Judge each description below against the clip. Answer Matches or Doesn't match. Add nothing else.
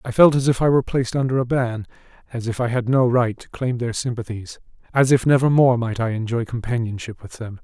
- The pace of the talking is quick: Matches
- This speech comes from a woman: Doesn't match